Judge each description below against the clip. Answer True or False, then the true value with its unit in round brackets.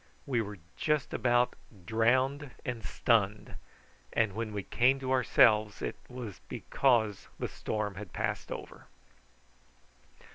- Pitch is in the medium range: False (115 Hz)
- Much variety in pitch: False (3.3 semitones)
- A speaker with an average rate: False (120 wpm)